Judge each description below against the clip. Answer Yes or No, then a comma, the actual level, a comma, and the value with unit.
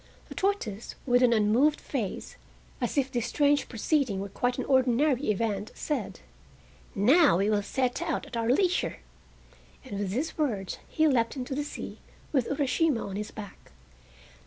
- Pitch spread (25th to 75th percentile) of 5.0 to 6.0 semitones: Yes, average, 5.3 semitones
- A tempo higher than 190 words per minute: No, average, 160 wpm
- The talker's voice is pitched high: Yes, high, 245 Hz